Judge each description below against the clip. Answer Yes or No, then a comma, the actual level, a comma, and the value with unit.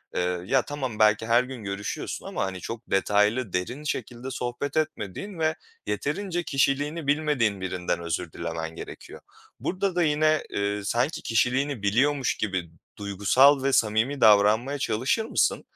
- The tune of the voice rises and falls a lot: Yes, wide, 6.0 semitones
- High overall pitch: No, low, 120 Hz